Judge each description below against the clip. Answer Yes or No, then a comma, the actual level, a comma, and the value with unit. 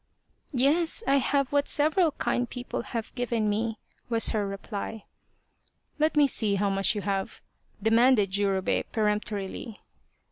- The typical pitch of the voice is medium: No, high, 225 Hz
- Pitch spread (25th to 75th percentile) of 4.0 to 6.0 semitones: Yes, average, 4.6 semitones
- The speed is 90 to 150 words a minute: Yes, average, 145 wpm